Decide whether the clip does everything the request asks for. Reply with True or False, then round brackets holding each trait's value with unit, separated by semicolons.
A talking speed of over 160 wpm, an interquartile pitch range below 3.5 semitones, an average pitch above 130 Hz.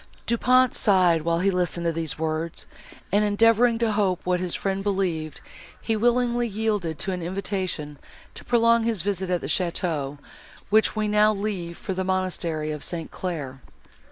False (170 wpm; 4.2 semitones; 185 Hz)